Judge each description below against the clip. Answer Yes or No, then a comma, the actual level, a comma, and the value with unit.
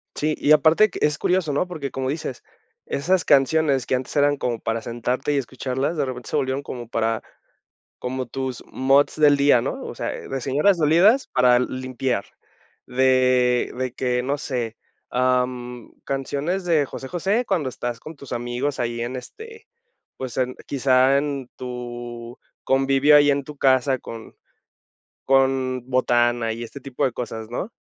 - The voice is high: No, low, 130 Hz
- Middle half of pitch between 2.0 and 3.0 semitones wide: Yes, average, 2.7 semitones